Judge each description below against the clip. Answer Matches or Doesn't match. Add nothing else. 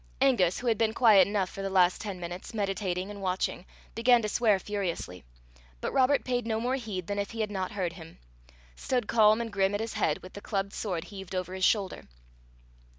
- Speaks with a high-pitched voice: Matches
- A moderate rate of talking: Doesn't match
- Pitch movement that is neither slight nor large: Matches